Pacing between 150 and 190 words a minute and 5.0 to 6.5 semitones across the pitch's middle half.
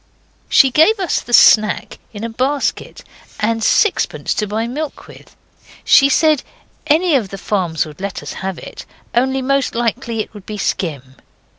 Yes: average, 165 wpm; average, 5.3 semitones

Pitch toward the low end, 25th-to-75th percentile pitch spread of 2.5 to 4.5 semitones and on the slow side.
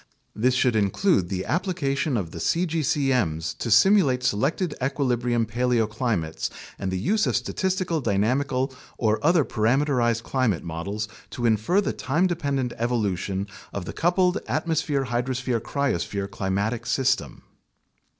No: low, 125 Hz; average, 5.3 semitones; slow, 130 wpm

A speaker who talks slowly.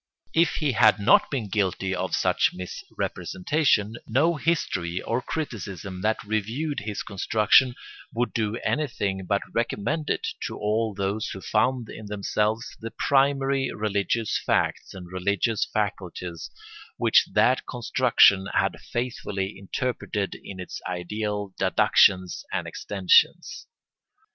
Yes: slow, 120 wpm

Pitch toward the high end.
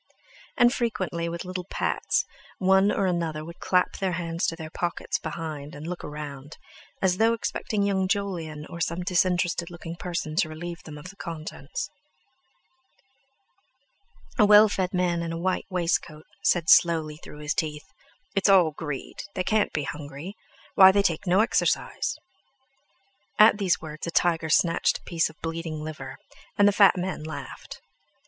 No: medium, 170 Hz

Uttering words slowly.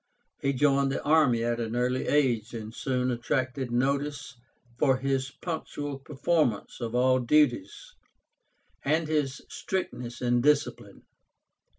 Yes: slow, 120 wpm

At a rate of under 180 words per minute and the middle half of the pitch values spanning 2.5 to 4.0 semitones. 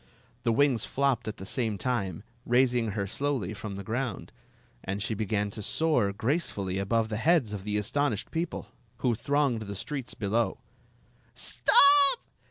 No: average, 160 wpm; average, 5.1 semitones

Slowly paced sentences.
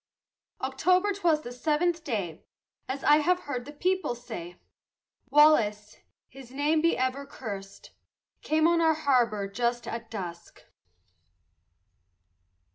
Yes: slow, 120 wpm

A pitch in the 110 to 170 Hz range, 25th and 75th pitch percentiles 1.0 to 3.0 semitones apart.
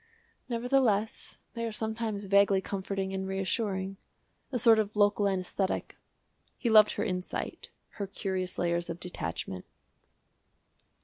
No: high, 200 Hz; narrow, 2.5 semitones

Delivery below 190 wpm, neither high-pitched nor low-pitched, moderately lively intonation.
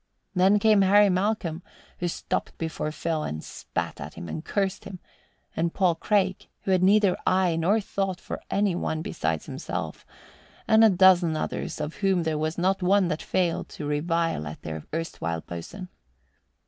Yes: average, 170 wpm; medium, 180 Hz; average, 3.5 semitones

